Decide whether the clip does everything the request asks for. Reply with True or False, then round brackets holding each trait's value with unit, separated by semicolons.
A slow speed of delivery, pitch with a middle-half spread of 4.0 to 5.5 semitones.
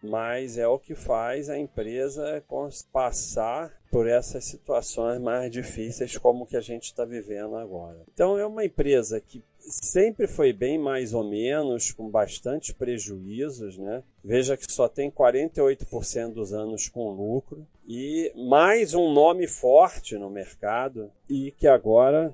False (145 wpm; 4.5 semitones)